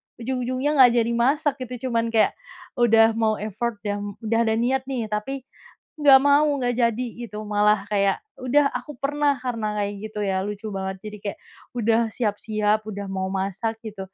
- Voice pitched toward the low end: No, high, 225 Hz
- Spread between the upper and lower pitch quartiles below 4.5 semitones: Yes, average, 3.3 semitones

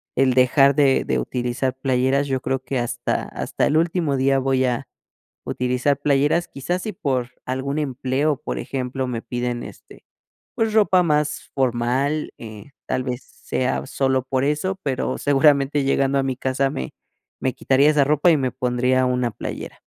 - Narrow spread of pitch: Yes, narrow, 2.1 semitones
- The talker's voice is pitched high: No, low, 135 Hz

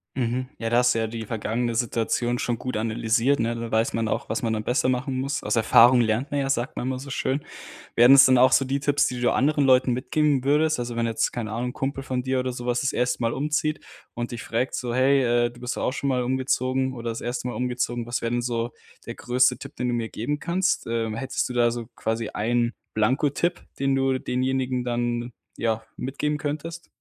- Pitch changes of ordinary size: No, narrow, 2.2 semitones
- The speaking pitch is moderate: No, low, 125 Hz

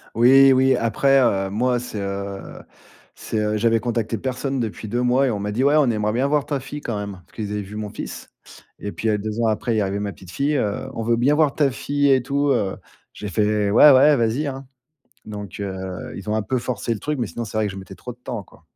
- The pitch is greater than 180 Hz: No, low, 115 Hz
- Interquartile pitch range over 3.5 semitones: Yes, average, 4.2 semitones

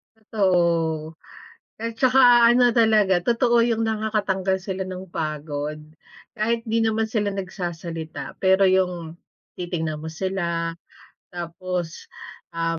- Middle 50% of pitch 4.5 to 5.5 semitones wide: Yes, average, 4.8 semitones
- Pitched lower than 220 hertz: Yes, high, 190 Hz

